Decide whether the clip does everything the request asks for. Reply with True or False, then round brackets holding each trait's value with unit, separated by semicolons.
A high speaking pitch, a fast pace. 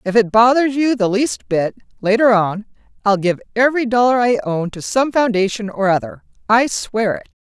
False (220 Hz; 185 wpm)